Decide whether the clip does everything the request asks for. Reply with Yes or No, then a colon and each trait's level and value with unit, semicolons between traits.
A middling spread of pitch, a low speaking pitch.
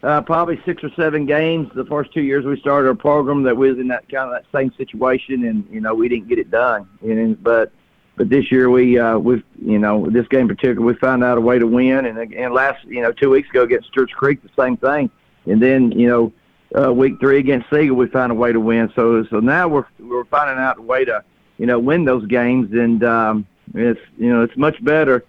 Yes: average, 3.6 semitones; low, 130 Hz